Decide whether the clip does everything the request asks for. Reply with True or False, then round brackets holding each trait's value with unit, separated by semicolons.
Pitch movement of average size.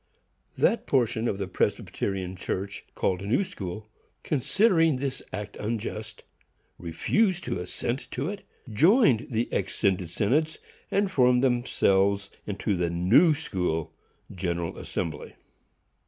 False (6.7 semitones)